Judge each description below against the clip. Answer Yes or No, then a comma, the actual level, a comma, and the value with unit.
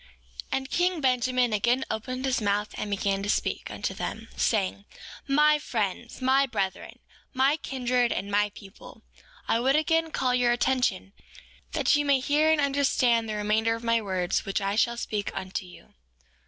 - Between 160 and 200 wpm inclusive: Yes, average, 175 wpm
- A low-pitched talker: No, high, 240 Hz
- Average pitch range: Yes, average, 4.5 semitones